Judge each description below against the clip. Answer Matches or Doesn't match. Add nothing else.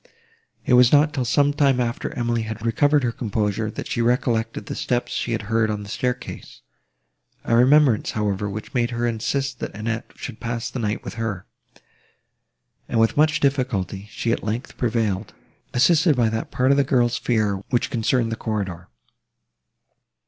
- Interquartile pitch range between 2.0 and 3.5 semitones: Matches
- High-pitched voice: Doesn't match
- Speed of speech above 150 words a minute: Matches